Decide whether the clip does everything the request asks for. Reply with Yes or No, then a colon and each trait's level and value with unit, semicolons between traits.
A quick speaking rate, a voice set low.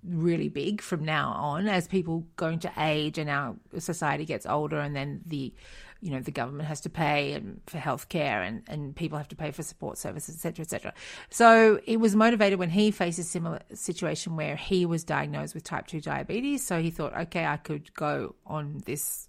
No: fast, 210 wpm; medium, 165 Hz